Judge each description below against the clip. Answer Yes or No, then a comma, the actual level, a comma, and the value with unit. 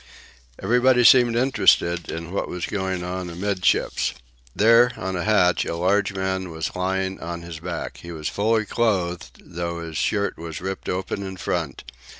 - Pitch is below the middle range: Yes, very low, 95 Hz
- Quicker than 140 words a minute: Yes, average, 165 wpm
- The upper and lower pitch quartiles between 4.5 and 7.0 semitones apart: No, average, 3.0 semitones